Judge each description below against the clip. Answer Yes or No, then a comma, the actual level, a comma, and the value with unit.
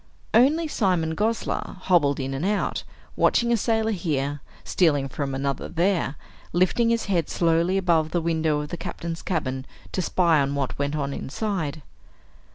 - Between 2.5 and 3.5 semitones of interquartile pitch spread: No, average, 5.1 semitones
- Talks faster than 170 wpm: No, average, 160 wpm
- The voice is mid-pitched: Yes, medium, 165 Hz